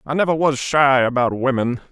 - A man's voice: Yes, male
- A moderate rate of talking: Yes, average, 190 wpm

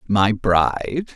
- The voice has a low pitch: Yes, low, 110 Hz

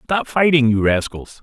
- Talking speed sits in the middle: Yes, average, 170 wpm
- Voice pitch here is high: No, low, 135 Hz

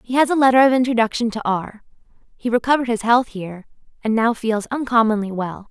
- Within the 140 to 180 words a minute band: No, average, 190 wpm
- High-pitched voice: Yes, high, 230 Hz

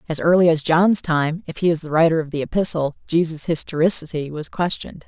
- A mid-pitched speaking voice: Yes, medium, 165 Hz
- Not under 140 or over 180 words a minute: No, average, 200 wpm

